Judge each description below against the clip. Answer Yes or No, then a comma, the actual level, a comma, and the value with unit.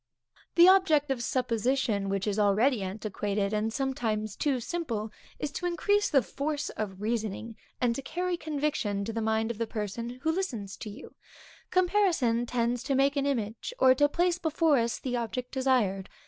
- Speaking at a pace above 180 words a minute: No, average, 175 wpm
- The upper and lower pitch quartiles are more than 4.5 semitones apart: Yes, average, 5.3 semitones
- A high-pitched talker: Yes, high, 245 Hz